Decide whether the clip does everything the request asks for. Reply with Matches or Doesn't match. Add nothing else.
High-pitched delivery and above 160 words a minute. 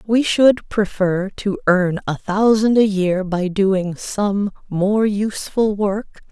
Doesn't match